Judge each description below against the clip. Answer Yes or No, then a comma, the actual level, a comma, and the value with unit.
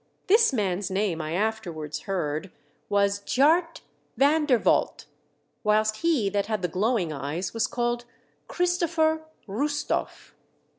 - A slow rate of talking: Yes, slow, 120 wpm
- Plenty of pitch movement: Yes, wide, 7.6 semitones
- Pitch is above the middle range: Yes, high, 215 Hz